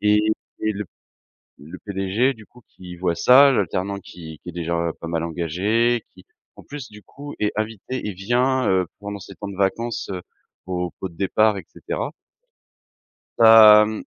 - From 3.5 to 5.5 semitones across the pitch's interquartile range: Yes, average, 3.8 semitones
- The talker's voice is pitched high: No, low, 100 Hz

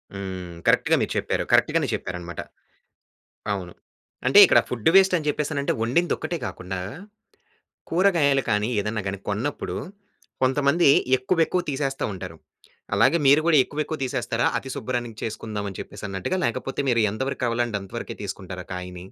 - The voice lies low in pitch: Yes, low, 120 Hz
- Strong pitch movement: Yes, wide, 6.8 semitones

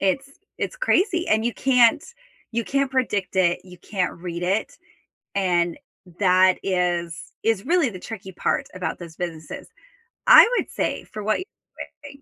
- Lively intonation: Yes, wide, 6.3 semitones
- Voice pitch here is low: No, high, 195 Hz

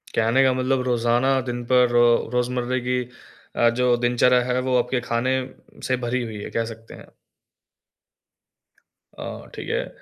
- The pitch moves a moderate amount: No, narrow, 1.3 semitones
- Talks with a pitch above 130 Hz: No, low, 125 Hz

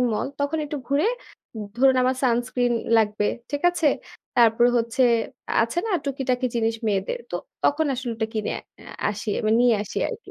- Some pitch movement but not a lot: Yes, average, 3.9 semitones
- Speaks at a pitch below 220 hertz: No, high, 245 Hz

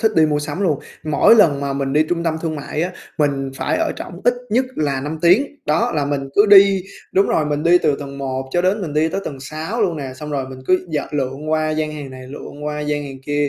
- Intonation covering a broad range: No, average, 3.6 semitones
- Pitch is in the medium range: Yes, medium, 150 Hz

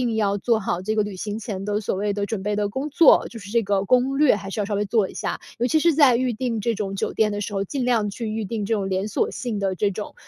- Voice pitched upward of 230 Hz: No, high, 210 Hz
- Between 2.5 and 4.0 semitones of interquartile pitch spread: Yes, average, 2.9 semitones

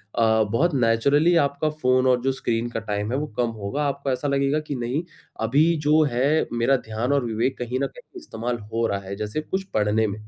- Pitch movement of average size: Yes, average, 3.9 semitones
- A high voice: No, low, 125 Hz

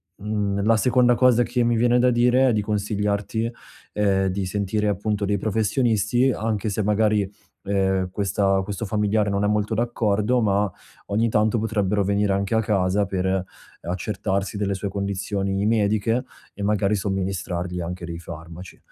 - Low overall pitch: Yes, low, 105 Hz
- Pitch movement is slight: Yes, narrow, 2.0 semitones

